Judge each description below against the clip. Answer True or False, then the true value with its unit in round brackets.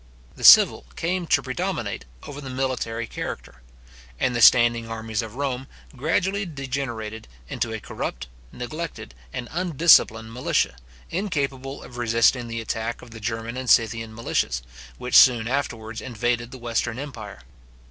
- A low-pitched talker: True (120 Hz)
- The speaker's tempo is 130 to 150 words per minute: True (140 wpm)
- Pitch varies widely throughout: False (3.2 semitones)